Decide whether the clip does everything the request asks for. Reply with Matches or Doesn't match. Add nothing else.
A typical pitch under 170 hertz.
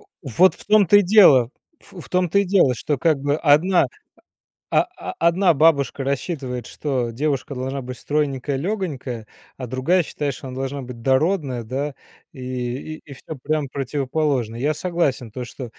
Matches